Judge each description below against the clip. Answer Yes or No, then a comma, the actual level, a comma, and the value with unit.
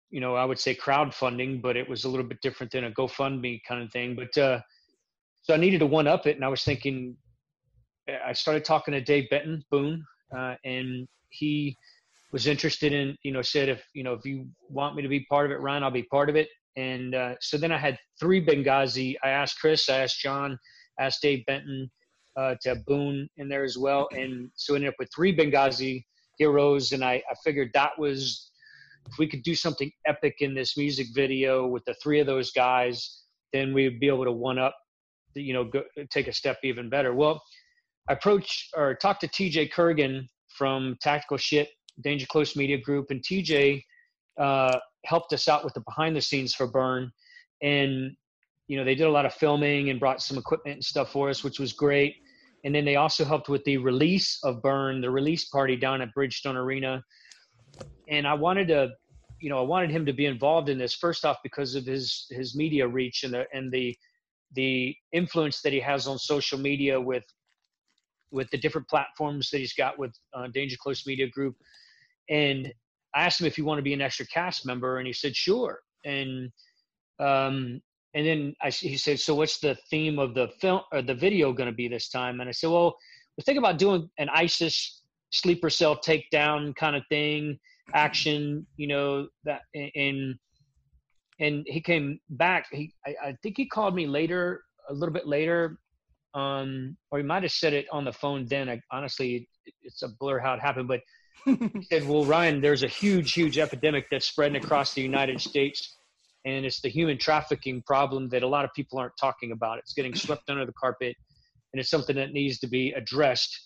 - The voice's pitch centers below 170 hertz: Yes, medium, 140 Hz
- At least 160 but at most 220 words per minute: Yes, fast, 205 wpm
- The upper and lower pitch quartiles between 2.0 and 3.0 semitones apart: Yes, narrow, 2.5 semitones